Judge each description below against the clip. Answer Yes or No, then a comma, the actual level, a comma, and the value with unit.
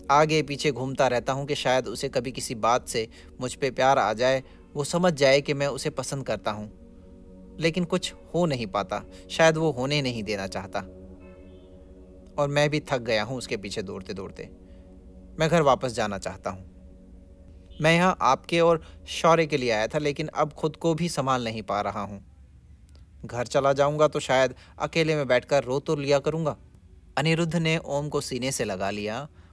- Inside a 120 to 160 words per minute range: No, fast, 190 wpm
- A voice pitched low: Yes, low, 130 Hz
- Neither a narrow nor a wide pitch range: No, wide, 8.2 semitones